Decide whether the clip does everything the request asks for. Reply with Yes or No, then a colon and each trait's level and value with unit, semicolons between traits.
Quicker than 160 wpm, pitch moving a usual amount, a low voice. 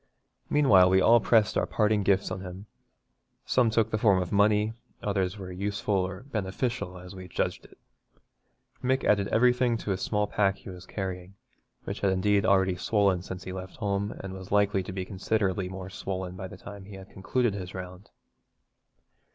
No: average, 185 wpm; narrow, 2.0 semitones; low, 100 Hz